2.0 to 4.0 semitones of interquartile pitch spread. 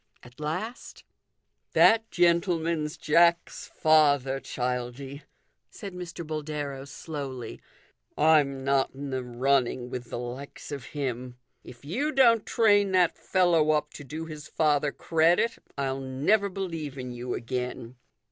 No: average, 4.4 semitones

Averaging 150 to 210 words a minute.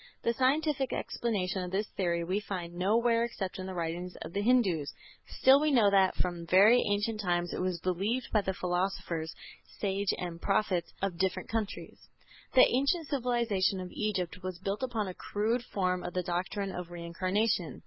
Yes: average, 175 wpm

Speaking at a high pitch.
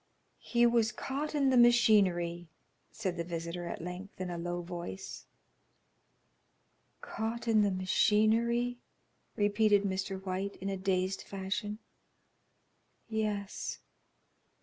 Yes: high, 200 Hz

